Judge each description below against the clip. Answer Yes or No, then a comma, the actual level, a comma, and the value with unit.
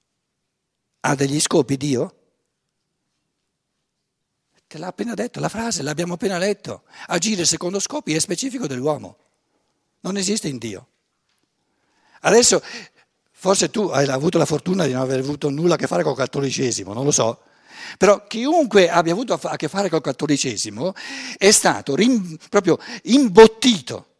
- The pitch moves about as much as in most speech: No, wide, 6.3 semitones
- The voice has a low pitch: No, medium, 170 Hz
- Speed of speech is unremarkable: Yes, average, 140 wpm